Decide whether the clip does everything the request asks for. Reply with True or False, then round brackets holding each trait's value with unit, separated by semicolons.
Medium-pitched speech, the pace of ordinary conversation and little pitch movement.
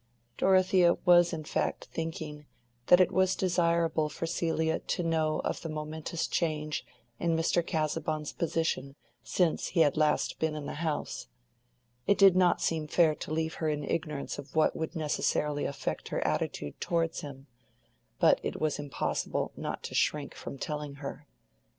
True (160 Hz; 160 wpm; 2.0 semitones)